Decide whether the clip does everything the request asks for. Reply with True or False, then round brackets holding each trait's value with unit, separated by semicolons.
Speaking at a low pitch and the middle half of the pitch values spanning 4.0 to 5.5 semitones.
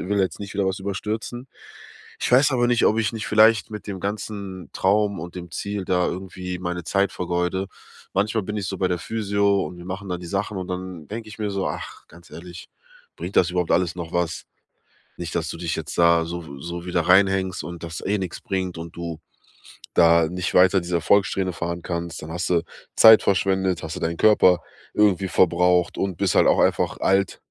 False (95 Hz; 2.5 semitones)